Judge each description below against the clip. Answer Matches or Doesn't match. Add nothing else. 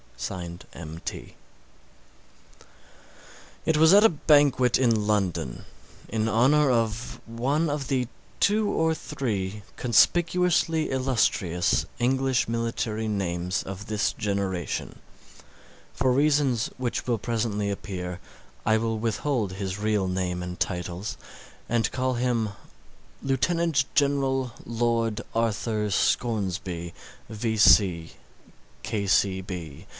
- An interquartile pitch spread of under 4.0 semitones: Doesn't match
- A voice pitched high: Doesn't match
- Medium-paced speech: Doesn't match